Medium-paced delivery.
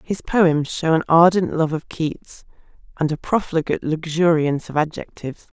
Yes: average, 150 wpm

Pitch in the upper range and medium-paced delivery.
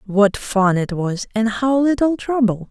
Yes: high, 225 Hz; average, 180 wpm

